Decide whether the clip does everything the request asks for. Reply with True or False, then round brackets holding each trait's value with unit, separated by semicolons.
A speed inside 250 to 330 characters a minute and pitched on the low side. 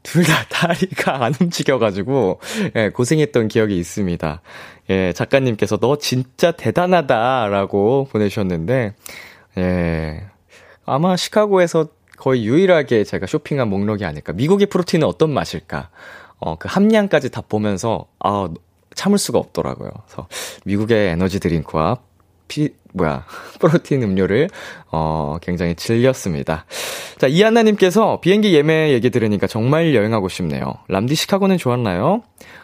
True (315 characters per minute; 120 Hz)